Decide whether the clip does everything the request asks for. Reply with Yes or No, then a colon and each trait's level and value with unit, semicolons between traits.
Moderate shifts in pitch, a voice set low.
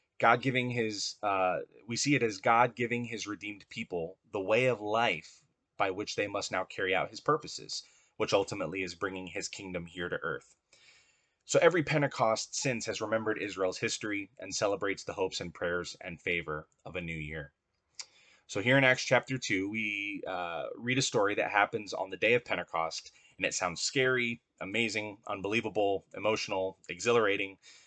Yes: average, 4.1 semitones; low, 105 Hz